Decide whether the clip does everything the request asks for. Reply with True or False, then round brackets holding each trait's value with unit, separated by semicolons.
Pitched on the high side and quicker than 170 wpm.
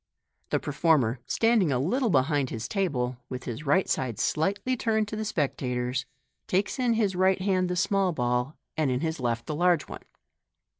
False (160 Hz; 185 wpm)